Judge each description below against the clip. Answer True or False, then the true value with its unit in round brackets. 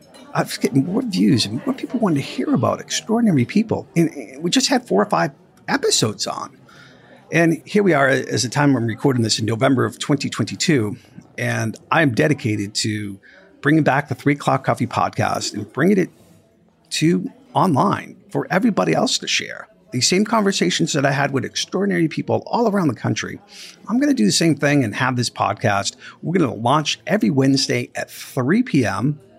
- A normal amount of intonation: False (6.9 semitones)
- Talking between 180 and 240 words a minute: True (185 wpm)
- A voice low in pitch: False (145 Hz)